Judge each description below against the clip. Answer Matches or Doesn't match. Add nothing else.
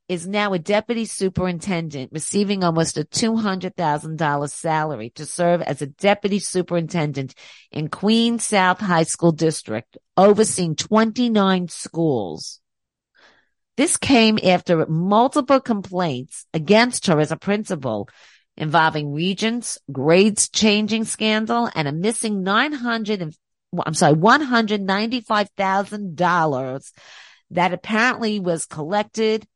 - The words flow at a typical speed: Doesn't match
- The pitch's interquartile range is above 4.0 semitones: Matches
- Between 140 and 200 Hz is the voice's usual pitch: Matches